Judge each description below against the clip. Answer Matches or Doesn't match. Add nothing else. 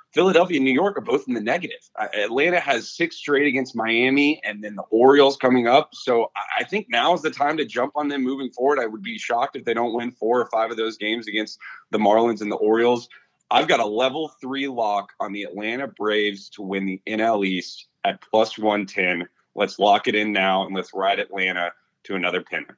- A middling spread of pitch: Matches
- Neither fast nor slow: Doesn't match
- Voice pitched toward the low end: Matches